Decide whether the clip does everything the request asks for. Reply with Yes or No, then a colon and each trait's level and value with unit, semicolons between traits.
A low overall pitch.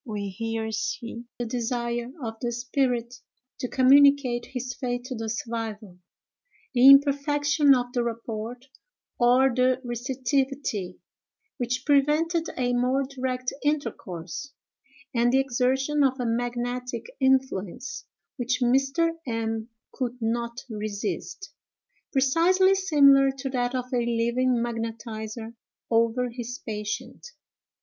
No: high, 245 Hz